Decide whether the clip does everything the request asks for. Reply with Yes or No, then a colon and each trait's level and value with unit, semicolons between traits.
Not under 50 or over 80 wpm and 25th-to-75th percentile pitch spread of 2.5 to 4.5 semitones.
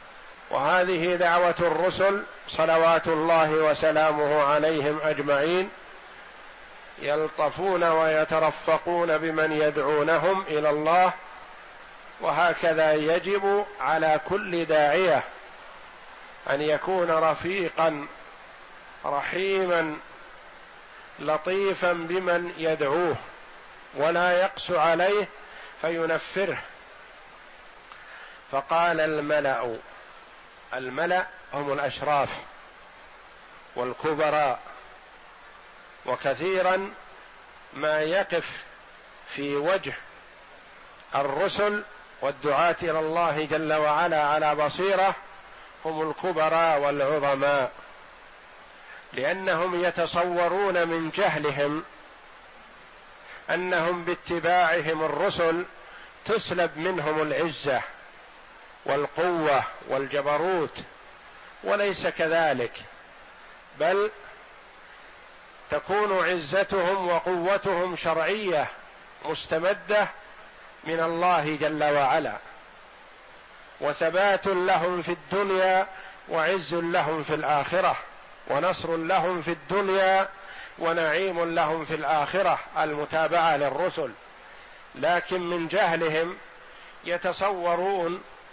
Yes: slow, 65 wpm; average, 2.9 semitones